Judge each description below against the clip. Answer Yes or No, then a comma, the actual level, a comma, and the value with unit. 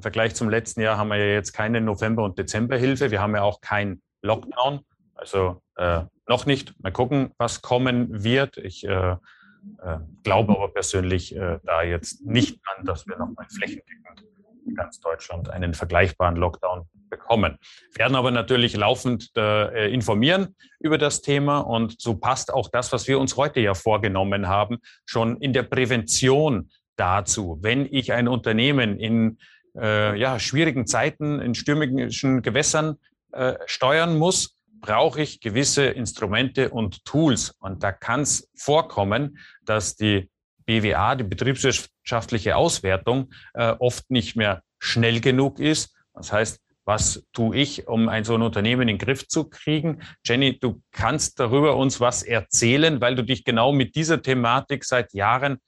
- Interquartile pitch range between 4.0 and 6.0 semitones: Yes, average, 4.5 semitones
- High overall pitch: No, low, 120 Hz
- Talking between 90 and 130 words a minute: No, average, 155 wpm